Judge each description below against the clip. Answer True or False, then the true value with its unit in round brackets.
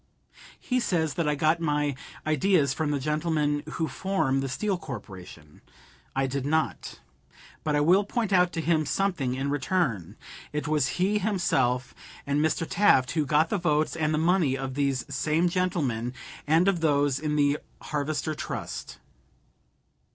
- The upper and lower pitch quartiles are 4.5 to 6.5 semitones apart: False (3.7 semitones)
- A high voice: False (150 Hz)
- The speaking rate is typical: True (160 wpm)